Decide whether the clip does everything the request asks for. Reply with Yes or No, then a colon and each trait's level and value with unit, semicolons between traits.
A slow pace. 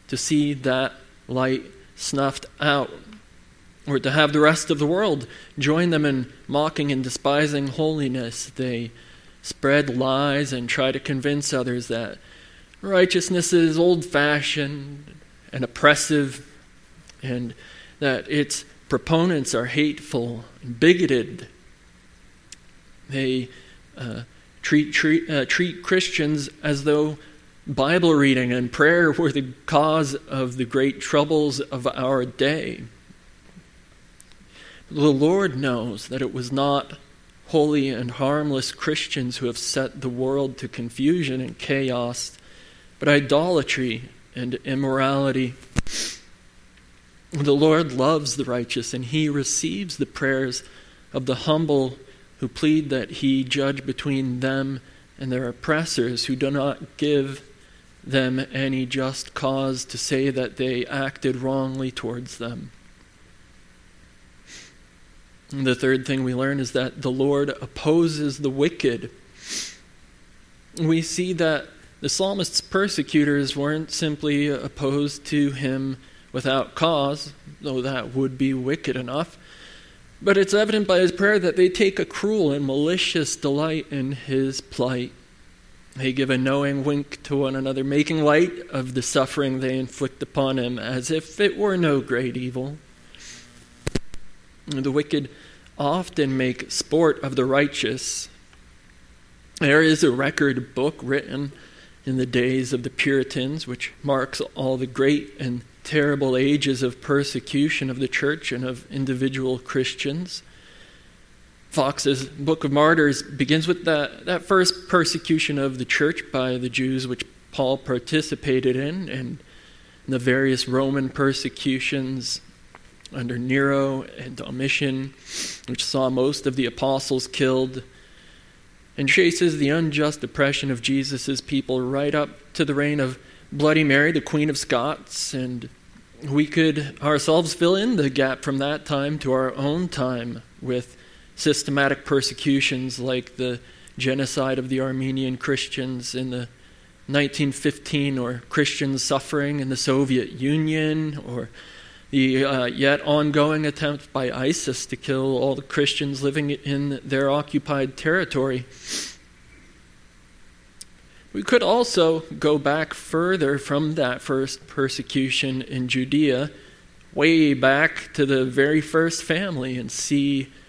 Yes: slow, 130 wpm